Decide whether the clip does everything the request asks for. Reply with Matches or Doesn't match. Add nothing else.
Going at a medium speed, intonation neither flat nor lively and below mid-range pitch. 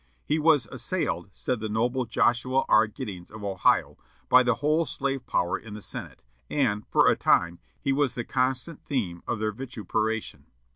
Matches